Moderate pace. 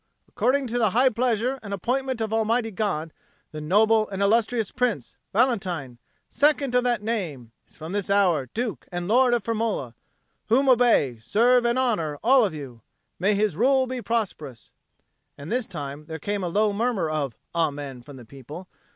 Yes: average, 175 wpm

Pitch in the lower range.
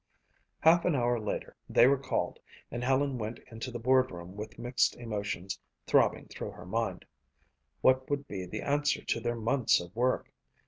Yes: low, 120 Hz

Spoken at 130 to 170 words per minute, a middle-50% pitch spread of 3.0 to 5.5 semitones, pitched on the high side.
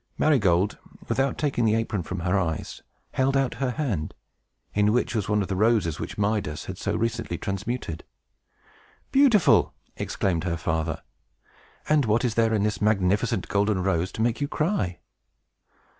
No: average, 160 wpm; average, 4.6 semitones; low, 105 Hz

